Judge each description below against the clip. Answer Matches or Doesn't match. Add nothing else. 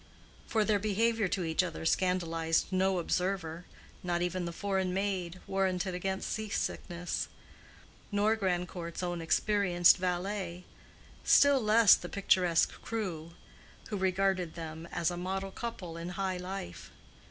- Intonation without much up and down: Matches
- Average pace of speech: Doesn't match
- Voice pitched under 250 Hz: Matches